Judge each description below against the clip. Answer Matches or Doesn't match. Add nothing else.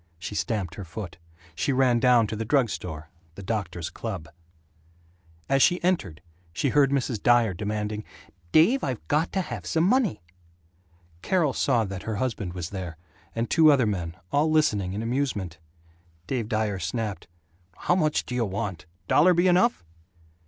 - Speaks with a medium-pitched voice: Doesn't match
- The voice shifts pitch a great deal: Matches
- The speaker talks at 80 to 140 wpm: Doesn't match